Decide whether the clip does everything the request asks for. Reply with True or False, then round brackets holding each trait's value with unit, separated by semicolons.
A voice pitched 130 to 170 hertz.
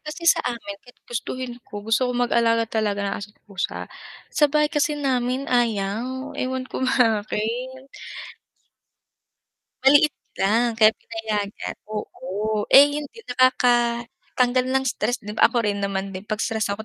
False (235 Hz)